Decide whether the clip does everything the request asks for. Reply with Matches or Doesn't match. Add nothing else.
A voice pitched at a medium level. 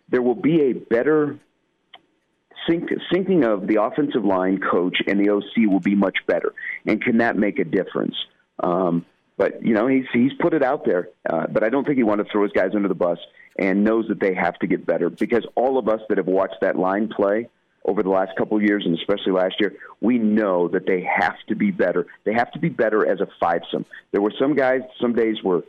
Doesn't match